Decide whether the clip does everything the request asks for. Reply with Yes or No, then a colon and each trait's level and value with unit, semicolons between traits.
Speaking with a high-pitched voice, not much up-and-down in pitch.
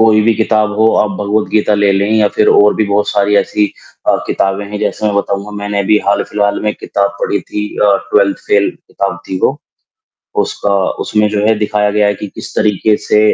No: low, 105 Hz; narrow, 0.9 semitones